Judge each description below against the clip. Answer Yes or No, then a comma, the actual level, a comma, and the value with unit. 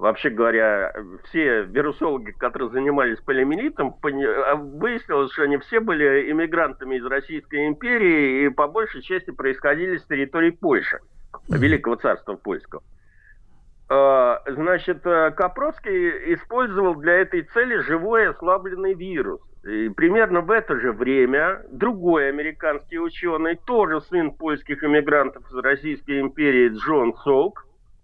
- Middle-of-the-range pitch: Yes, medium, 160 Hz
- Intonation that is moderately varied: No, wide, 7.3 semitones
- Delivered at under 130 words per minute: Yes, average, 120 wpm